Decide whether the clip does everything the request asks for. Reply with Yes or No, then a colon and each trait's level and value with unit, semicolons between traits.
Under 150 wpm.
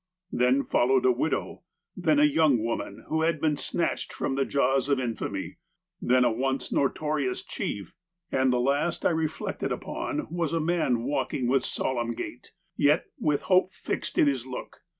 No: average, 170 wpm